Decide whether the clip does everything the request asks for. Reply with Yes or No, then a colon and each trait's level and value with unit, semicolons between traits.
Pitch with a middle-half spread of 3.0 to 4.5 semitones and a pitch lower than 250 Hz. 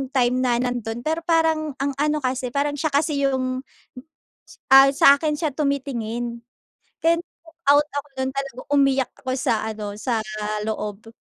No: average, 3.4 semitones; very high, 275 Hz